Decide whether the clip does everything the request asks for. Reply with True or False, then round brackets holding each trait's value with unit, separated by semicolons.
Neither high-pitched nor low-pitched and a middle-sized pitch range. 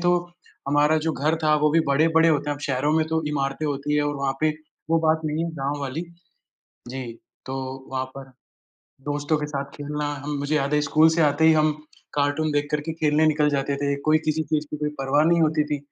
False (150 Hz; 1.6 semitones)